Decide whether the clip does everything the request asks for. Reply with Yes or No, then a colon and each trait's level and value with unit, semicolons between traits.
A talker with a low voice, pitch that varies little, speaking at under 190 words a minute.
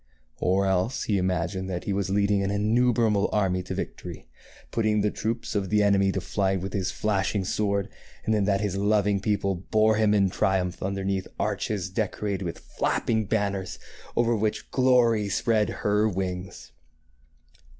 Yes: low, 100 Hz; narrow, 1.9 semitones; average, 160 wpm